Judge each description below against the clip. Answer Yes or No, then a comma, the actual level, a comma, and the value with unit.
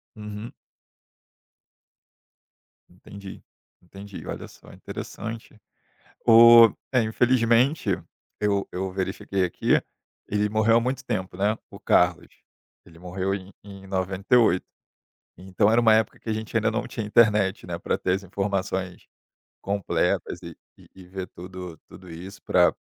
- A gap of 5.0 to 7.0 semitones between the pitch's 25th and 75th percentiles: No, average, 2.9 semitones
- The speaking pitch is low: Yes, low, 100 Hz